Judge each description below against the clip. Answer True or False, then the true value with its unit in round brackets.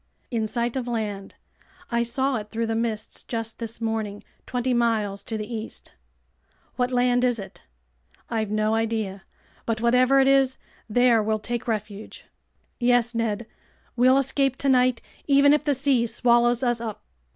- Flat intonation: True (2.2 semitones)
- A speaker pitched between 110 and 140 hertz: False (235 Hz)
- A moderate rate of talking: True (155 wpm)